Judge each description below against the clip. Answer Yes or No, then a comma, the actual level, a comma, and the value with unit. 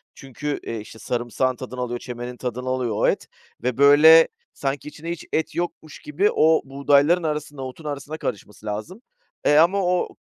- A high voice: No, medium, 140 Hz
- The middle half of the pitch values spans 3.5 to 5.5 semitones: Yes, average, 4.0 semitones